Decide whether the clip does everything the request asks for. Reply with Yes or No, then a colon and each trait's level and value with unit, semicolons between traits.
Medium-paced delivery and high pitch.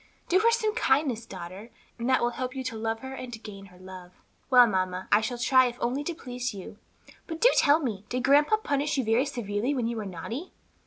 No: fast, 230 wpm; high, 245 Hz